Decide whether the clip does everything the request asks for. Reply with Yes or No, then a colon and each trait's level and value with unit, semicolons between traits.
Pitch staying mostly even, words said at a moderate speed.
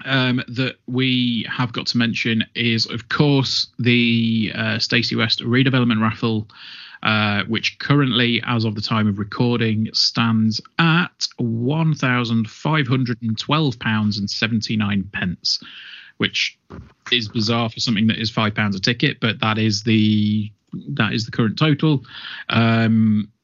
Yes: narrow, 2.3 semitones; average, 150 wpm